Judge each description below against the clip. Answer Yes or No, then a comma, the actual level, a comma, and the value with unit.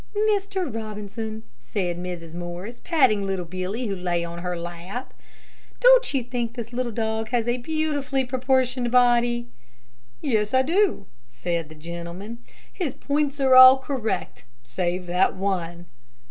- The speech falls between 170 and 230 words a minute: No, average, 145 wpm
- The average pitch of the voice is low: No, high, 225 Hz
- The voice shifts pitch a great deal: Yes, wide, 6.4 semitones